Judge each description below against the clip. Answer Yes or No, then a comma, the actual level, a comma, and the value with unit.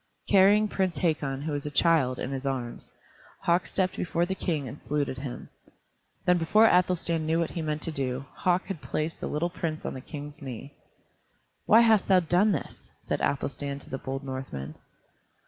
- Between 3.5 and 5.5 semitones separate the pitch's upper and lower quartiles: Yes, average, 4.6 semitones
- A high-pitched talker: No, medium, 155 Hz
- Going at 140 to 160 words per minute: No, average, 185 wpm